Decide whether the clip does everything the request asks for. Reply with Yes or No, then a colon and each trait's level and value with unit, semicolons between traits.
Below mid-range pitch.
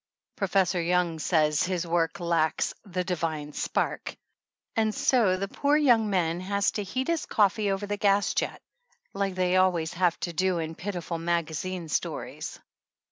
No: medium, 185 Hz